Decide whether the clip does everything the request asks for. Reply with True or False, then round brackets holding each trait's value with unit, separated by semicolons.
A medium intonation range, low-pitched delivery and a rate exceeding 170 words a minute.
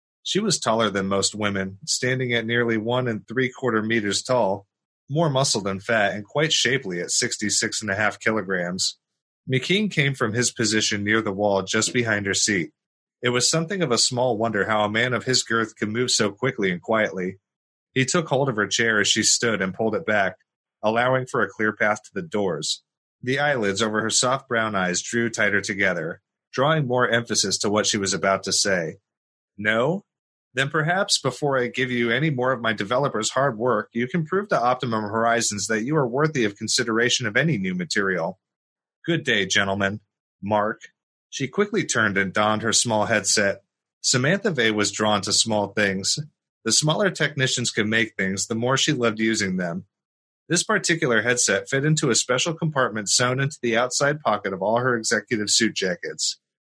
True (4.0 semitones; 115 Hz; 190 wpm)